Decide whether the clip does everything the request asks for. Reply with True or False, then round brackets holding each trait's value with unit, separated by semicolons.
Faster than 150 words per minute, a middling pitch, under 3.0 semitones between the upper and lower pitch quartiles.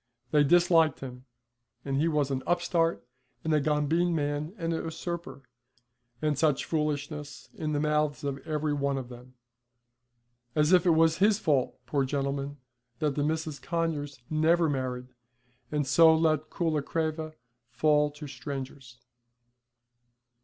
False (140 wpm; 150 Hz; 2.4 semitones)